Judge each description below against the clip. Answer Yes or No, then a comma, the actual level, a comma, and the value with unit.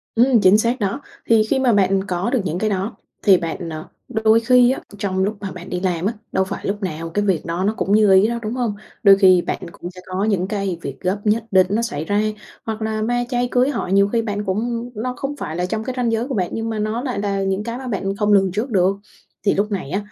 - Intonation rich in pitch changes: No, average, 3.3 semitones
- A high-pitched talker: Yes, high, 205 Hz